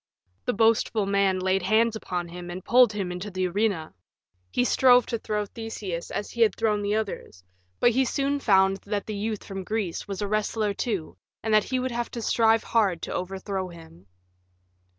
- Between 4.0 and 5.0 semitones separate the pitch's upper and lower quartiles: No, average, 3.1 semitones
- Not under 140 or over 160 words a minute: No, average, 190 wpm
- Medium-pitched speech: No, high, 205 Hz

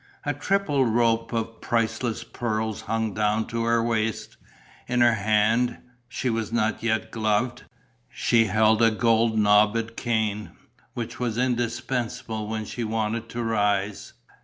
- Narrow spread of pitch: Yes, narrow, 1.5 semitones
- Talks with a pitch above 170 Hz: No, low, 115 Hz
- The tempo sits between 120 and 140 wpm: Yes, slow, 135 wpm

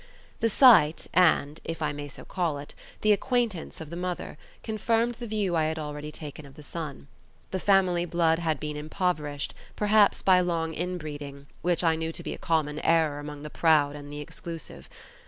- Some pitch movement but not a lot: Yes, average, 3.5 semitones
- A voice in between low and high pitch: Yes, medium, 160 Hz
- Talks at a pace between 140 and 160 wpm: No, average, 190 wpm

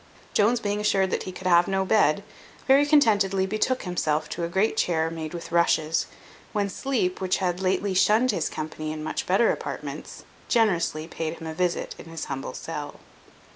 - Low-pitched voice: No, medium, 185 Hz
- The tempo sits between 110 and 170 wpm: No, average, 180 wpm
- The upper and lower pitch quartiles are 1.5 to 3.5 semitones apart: No, average, 4.0 semitones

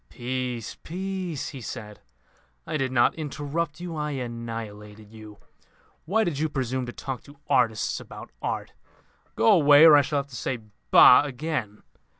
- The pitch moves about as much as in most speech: Yes, average, 4.8 semitones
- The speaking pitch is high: No, low, 135 Hz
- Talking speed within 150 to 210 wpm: Yes, average, 160 wpm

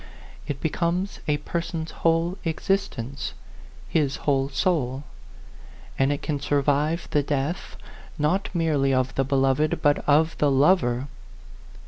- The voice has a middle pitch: Yes, medium, 145 Hz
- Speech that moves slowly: Yes, slow, 120 wpm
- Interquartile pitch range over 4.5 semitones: No, average, 3.3 semitones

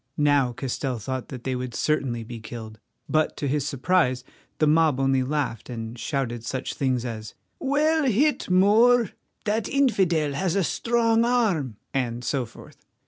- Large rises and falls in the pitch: Yes, wide, 7.8 semitones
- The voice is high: No, medium, 140 Hz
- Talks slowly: No, average, 155 wpm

